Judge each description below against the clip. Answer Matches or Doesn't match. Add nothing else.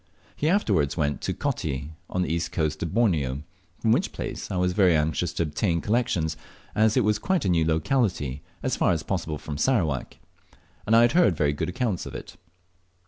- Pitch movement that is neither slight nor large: Doesn't match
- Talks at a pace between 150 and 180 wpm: Doesn't match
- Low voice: Matches